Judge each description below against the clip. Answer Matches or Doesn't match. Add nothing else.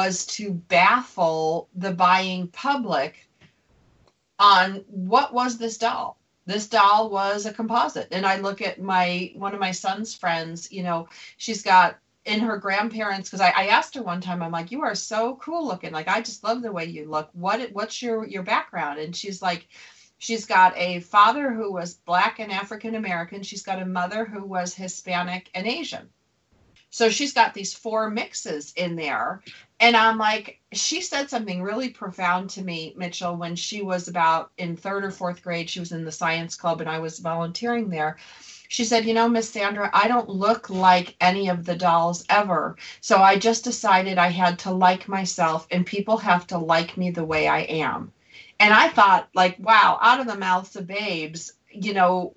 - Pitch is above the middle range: Matches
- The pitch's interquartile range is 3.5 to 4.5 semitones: Matches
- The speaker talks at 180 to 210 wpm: Matches